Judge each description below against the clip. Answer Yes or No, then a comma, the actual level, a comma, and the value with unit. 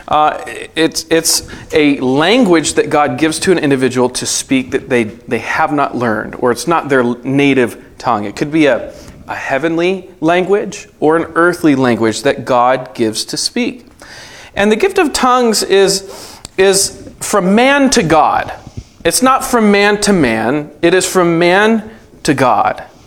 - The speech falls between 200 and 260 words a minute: No, average, 165 wpm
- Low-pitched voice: No, medium, 165 Hz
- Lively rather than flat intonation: Yes, wide, 6.9 semitones